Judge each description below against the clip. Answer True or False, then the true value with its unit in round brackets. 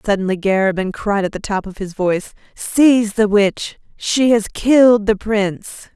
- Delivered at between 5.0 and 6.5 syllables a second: False (4.7 syllables/s)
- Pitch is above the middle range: True (205 Hz)